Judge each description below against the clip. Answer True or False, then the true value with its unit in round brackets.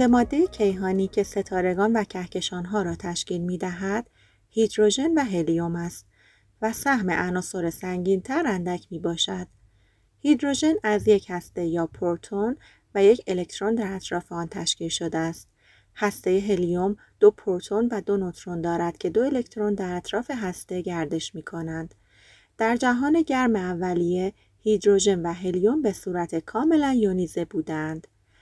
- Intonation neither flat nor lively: True (3.8 semitones)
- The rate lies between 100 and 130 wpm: False (140 wpm)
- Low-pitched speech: False (185 Hz)